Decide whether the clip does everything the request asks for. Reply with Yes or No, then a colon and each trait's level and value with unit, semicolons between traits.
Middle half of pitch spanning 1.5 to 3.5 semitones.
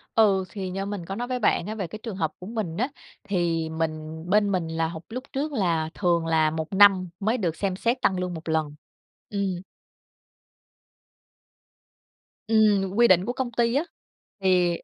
No: average, 4.6 semitones